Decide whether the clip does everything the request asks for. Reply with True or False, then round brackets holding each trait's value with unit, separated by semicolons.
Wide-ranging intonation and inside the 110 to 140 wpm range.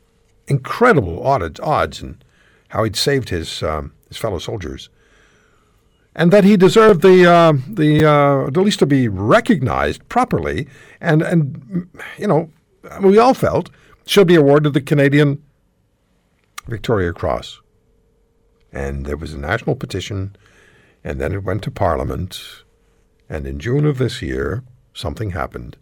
True (8.6 semitones; 135 wpm)